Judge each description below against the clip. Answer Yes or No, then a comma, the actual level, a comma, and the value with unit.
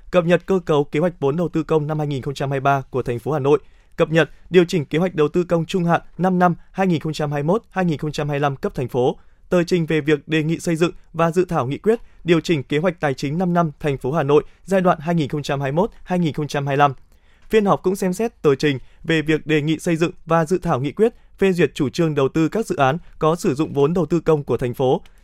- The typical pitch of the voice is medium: Yes, medium, 160 Hz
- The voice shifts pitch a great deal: No, average, 3.5 semitones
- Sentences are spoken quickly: No, average, 235 wpm